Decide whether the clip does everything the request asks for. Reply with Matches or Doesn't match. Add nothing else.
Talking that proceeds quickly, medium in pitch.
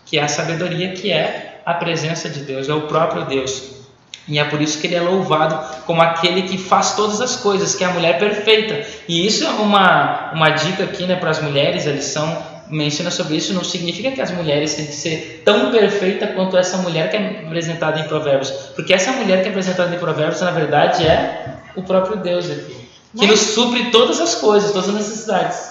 Matches